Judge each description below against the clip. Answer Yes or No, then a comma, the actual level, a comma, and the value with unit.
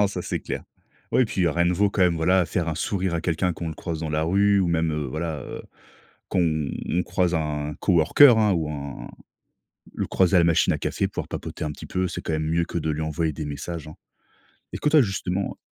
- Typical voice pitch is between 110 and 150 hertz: No, very low, 85 Hz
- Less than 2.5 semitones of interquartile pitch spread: No, average, 2.9 semitones